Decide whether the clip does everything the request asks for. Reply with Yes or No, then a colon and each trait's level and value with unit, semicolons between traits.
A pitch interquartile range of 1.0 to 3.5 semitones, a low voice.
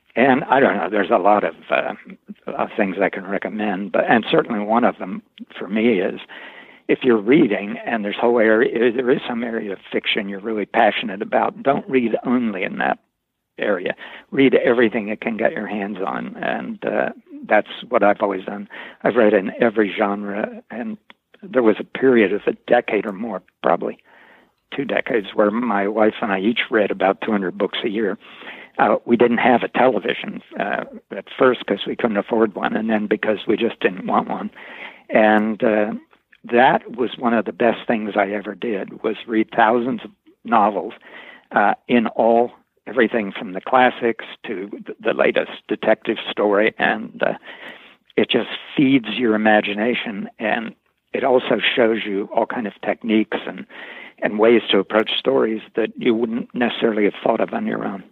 Yes: average, 3.2 semitones; low, 115 Hz